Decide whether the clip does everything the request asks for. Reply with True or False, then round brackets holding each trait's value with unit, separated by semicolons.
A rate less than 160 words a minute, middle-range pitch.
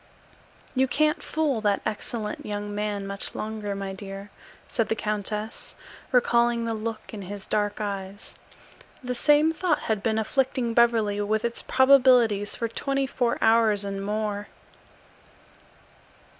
False (135 wpm; 220 Hz)